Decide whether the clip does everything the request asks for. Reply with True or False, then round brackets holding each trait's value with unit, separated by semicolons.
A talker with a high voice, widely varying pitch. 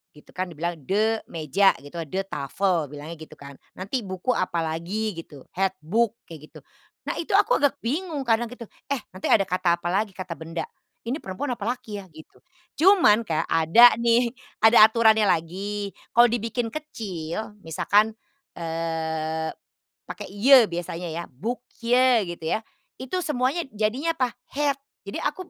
True (205 Hz; 6.2 semitones)